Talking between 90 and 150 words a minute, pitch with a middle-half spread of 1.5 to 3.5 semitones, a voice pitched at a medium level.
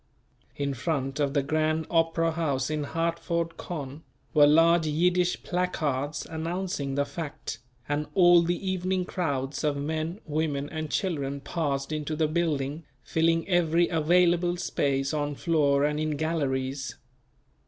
Yes: slow, 135 wpm; average, 2.9 semitones; medium, 155 Hz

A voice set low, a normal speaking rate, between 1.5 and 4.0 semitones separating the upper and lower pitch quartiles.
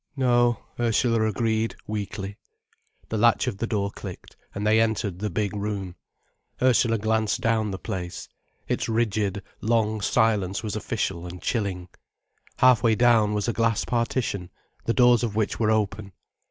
Yes: low, 110 Hz; average, 155 wpm; narrow, 2.4 semitones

